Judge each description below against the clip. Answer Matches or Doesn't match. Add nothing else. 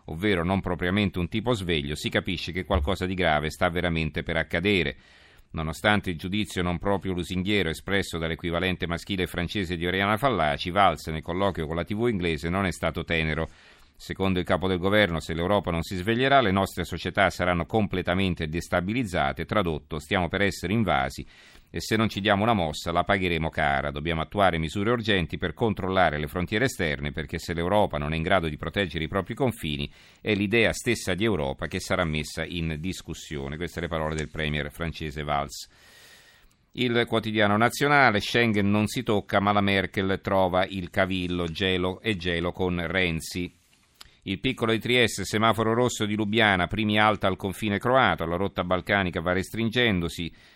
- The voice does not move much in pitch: Doesn't match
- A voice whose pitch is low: Matches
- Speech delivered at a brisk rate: Matches